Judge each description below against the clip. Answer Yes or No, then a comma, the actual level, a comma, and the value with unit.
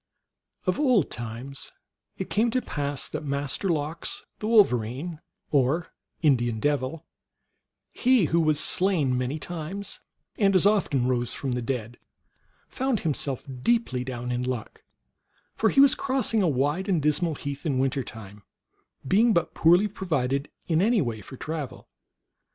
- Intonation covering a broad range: Yes, wide, 6.8 semitones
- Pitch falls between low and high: Yes, medium, 150 Hz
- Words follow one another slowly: No, average, 150 wpm